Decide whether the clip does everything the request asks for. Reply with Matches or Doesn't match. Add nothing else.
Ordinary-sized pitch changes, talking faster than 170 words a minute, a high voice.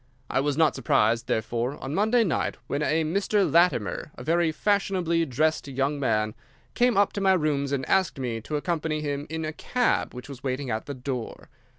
Doesn't match